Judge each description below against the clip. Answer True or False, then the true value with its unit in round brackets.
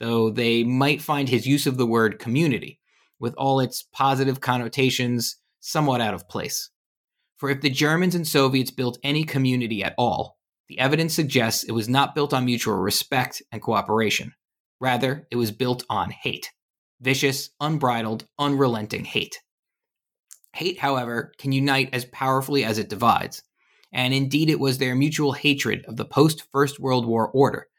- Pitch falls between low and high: False (130 Hz)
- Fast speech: False (160 wpm)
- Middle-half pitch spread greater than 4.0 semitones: False (2.8 semitones)